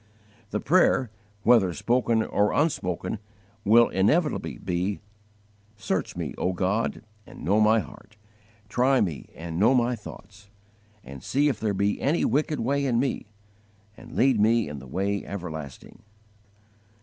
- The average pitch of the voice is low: Yes, low, 105 Hz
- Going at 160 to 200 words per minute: No, average, 140 wpm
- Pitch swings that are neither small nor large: Yes, average, 4.6 semitones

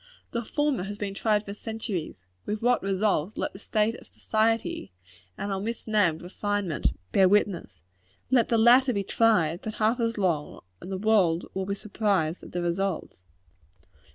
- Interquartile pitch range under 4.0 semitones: Yes, average, 3.2 semitones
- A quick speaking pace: No, average, 165 wpm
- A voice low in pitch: No, high, 205 Hz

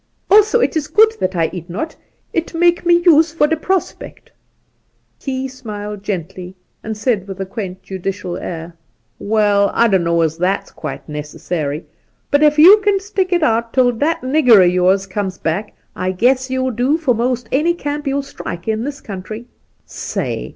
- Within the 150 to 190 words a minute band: Yes, average, 180 wpm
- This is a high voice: Yes, high, 230 Hz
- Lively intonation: Yes, wide, 8.2 semitones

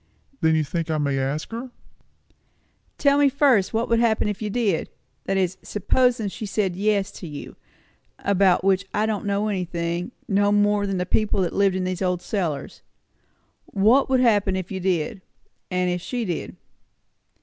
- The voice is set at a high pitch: Yes, high, 195 Hz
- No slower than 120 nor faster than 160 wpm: No, average, 170 wpm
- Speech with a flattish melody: No, average, 3.1 semitones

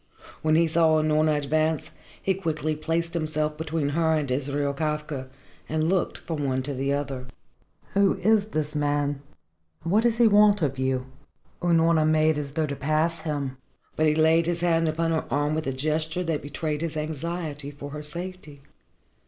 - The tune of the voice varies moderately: No, narrow, 2.3 semitones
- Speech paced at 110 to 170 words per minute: No, average, 185 wpm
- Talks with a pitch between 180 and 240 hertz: No, medium, 155 Hz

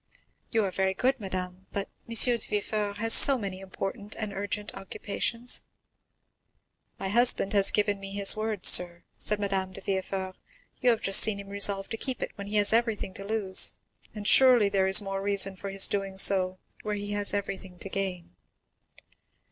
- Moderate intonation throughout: No, narrow, 1.6 semitones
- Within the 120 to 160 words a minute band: No, average, 180 wpm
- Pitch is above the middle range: Yes, high, 200 Hz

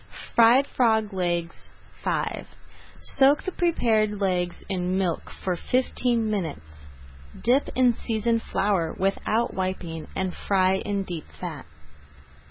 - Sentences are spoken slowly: Yes, slow, 115 wpm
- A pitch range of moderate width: Yes, average, 4.5 semitones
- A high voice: Yes, high, 195 Hz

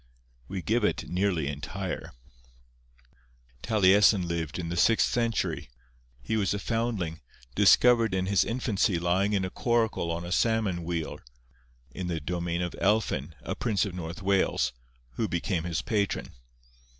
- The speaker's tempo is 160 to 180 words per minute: No, average, 145 wpm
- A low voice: Yes, very low, 95 Hz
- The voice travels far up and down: No, average, 3.8 semitones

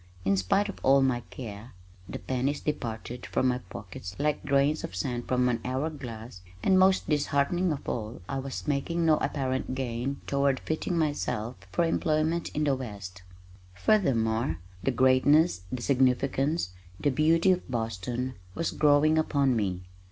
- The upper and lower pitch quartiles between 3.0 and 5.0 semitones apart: Yes, average, 4.3 semitones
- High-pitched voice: No, low, 135 Hz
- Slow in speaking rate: No, average, 155 wpm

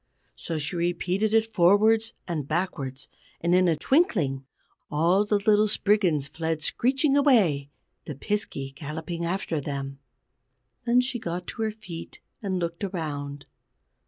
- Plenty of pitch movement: Yes, wide, 5.8 semitones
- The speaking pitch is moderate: Yes, medium, 175 Hz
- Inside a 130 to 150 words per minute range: Yes, slow, 135 wpm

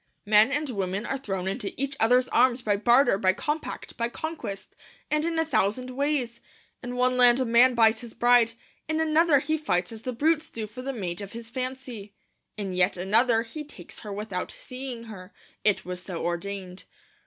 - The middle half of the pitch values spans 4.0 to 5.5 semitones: Yes, average, 4.7 semitones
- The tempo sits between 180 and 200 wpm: Yes, average, 190 wpm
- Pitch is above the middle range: Yes, high, 235 Hz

